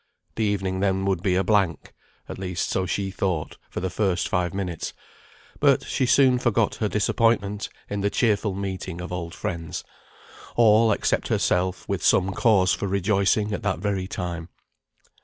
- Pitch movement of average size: No, narrow, 2.1 semitones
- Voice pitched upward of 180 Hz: No, very low, 95 Hz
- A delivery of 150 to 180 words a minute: Yes, average, 165 wpm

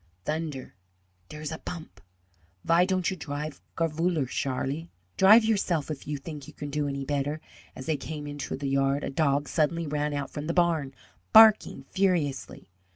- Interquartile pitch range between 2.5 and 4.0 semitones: Yes, average, 3.0 semitones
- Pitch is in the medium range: Yes, medium, 150 Hz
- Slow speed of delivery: No, average, 165 wpm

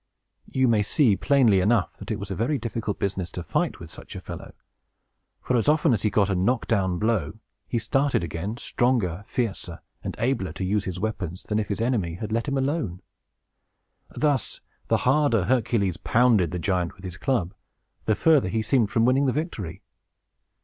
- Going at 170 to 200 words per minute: Yes, average, 190 wpm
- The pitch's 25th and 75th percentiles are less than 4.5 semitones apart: No, average, 5.3 semitones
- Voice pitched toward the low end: Yes, low, 110 Hz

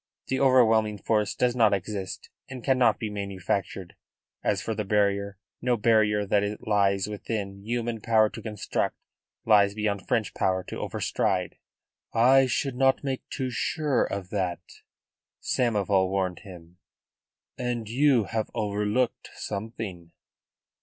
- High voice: No, low, 105 Hz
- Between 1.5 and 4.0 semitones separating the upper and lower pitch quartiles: Yes, average, 3.2 semitones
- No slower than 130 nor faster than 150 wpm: Yes, slow, 135 wpm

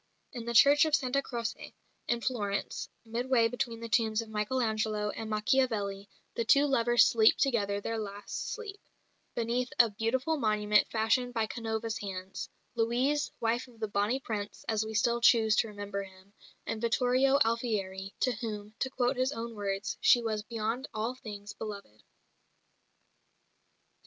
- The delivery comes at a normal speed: Yes, average, 155 wpm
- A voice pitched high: Yes, high, 225 Hz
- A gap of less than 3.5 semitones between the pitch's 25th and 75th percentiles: Yes, average, 2.7 semitones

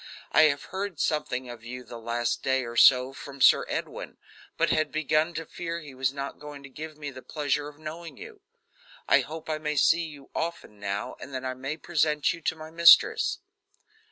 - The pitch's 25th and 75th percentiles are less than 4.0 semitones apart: Yes, average, 3.4 semitones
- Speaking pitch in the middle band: Yes, medium, 150 Hz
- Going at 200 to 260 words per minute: Yes, fast, 205 wpm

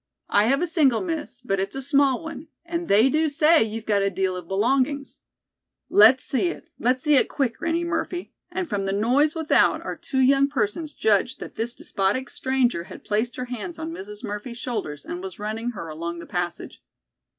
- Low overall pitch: No, very high, 250 Hz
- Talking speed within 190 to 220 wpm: Yes, average, 200 wpm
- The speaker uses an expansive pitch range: Yes, wide, 6.3 semitones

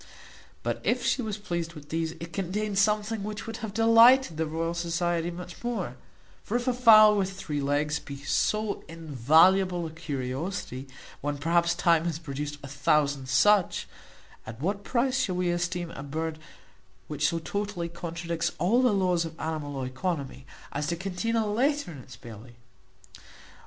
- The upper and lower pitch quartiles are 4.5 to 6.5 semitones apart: Yes, average, 5.3 semitones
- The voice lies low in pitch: No, medium, 170 Hz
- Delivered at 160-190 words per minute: Yes, average, 165 wpm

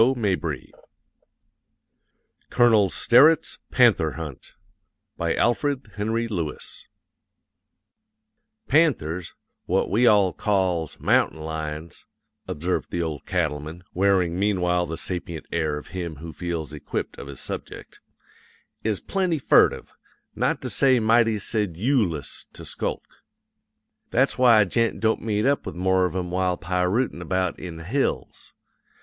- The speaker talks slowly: Yes, slow, 125 wpm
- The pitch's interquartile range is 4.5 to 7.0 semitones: Yes, average, 5.3 semitones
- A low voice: Yes, very low, 95 Hz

